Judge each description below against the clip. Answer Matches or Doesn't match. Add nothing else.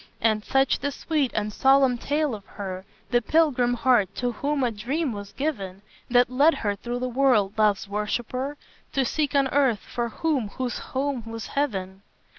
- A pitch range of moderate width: Matches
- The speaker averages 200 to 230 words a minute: Doesn't match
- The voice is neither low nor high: Doesn't match